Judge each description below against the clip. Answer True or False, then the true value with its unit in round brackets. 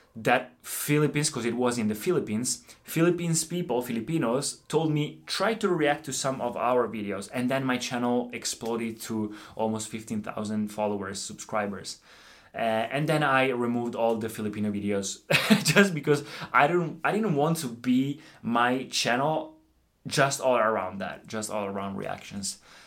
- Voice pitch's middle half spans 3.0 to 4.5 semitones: False (5.2 semitones)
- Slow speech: False (155 wpm)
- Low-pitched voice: True (120 Hz)